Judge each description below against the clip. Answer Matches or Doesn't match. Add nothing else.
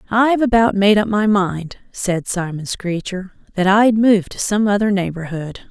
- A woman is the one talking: Matches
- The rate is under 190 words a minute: Matches